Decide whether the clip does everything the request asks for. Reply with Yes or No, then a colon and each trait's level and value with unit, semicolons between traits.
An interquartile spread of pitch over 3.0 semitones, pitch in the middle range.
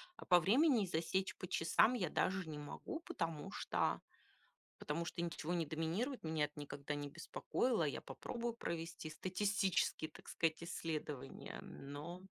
Yes: average, 3.7 semitones; medium, 170 Hz